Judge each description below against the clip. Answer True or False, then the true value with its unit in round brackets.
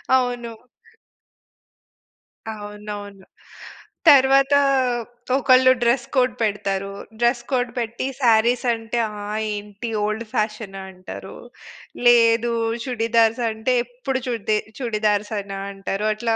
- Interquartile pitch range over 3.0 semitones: False (2.7 semitones)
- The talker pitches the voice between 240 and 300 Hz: False (225 Hz)